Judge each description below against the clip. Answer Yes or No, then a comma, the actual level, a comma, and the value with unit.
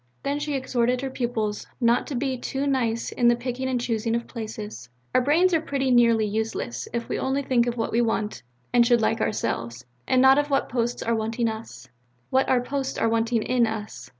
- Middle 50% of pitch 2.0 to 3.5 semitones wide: Yes, average, 2.8 semitones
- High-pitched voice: Yes, high, 240 Hz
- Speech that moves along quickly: Yes, fast, 210 wpm